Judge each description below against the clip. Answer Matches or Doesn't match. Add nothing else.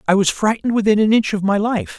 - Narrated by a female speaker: Doesn't match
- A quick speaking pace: Matches